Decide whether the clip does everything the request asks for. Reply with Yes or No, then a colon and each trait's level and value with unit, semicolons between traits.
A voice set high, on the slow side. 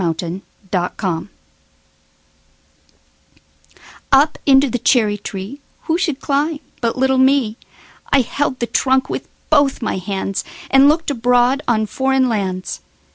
Yes: very high, 260 Hz; slow, 115 wpm